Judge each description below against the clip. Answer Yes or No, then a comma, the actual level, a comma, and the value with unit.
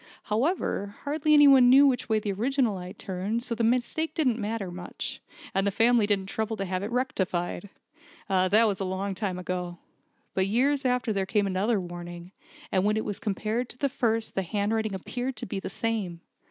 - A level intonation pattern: No, average, 4.3 semitones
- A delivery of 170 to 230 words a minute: Yes, average, 195 wpm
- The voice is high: Yes, high, 210 Hz